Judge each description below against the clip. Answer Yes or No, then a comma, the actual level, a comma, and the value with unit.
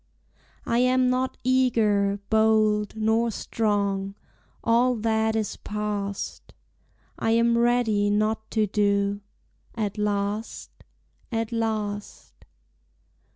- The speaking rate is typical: No, slow, 95 wpm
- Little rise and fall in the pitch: Yes, narrow, 2.0 semitones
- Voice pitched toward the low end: No, high, 220 Hz